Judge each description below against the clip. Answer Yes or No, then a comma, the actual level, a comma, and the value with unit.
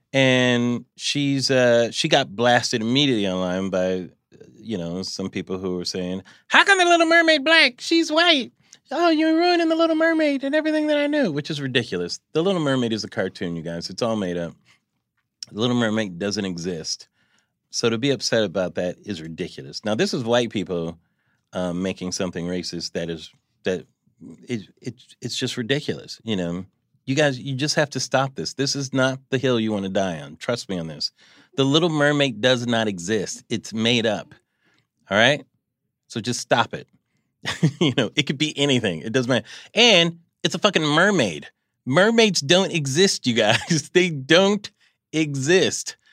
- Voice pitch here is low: Yes, low, 130 Hz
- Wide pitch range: Yes, wide, 9.0 semitones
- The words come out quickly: No, average, 185 wpm